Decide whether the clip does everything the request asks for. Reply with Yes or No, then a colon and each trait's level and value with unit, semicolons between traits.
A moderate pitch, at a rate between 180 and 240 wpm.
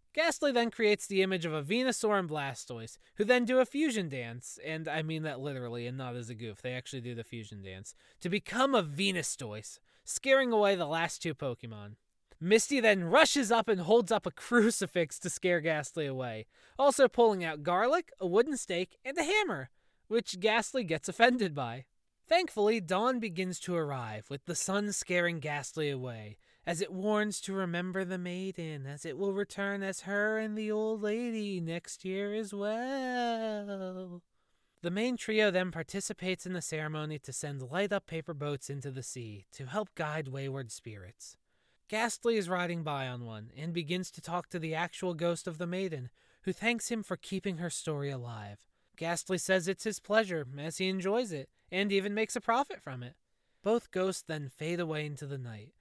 Yes: medium, 180 Hz; average, 185 wpm